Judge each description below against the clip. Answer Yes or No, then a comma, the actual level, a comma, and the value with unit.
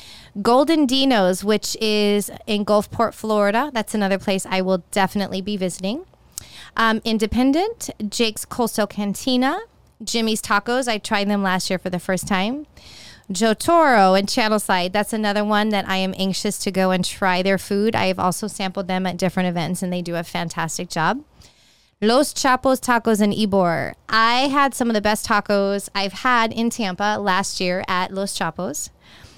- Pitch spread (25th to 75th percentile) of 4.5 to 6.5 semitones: No, average, 3.1 semitones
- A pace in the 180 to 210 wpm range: No, average, 170 wpm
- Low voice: No, high, 205 Hz